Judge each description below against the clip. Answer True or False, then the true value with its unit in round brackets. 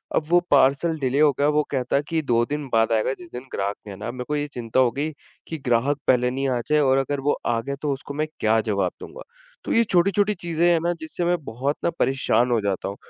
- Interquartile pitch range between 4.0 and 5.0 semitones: True (4.3 semitones)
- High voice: False (140 Hz)